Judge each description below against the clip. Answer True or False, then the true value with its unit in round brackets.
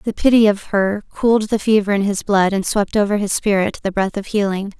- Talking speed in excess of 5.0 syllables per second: True (5.6 syllables/s)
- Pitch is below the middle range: False (205 Hz)